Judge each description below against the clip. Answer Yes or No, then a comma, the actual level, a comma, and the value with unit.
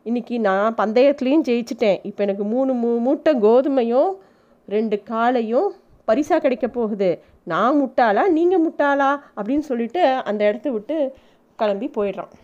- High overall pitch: Yes, high, 240 Hz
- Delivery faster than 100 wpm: Yes, average, 125 wpm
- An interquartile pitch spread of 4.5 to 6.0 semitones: Yes, average, 5.2 semitones